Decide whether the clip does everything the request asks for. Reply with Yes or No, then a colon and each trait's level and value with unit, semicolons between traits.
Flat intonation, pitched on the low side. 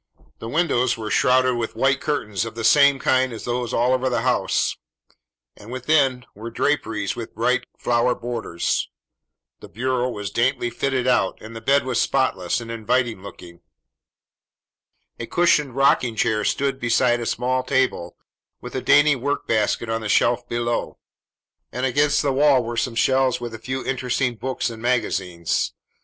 Yes: narrow, 2.3 semitones; low, 125 Hz